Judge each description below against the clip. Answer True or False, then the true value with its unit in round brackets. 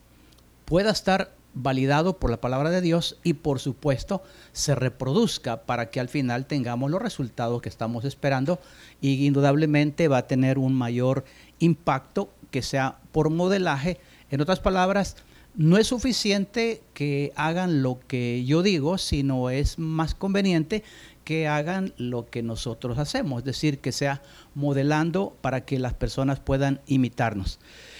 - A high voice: False (140 Hz)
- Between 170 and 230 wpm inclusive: False (145 wpm)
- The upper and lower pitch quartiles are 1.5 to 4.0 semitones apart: False (4.6 semitones)